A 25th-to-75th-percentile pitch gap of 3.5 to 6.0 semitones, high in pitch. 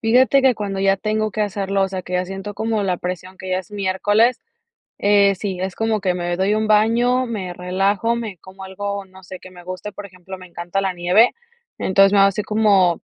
No: narrow, 2.4 semitones; high, 195 Hz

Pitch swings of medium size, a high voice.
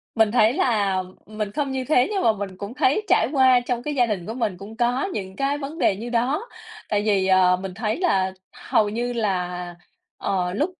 Yes: average, 4.9 semitones; high, 220 Hz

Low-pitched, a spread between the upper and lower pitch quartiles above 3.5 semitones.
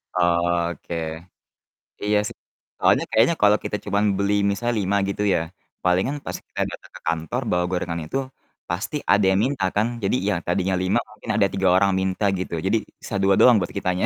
No: very low, 95 Hz; average, 2.8 semitones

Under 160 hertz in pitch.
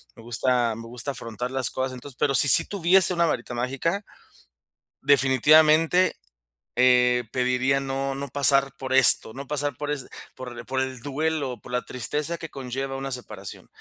Yes: low, 135 Hz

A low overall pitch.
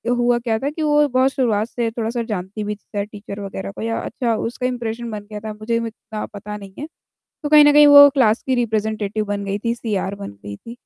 No: high, 220 Hz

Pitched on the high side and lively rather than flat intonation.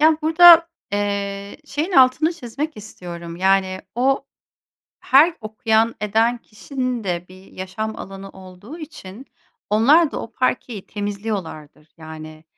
Yes: high, 215 Hz; wide, 6.0 semitones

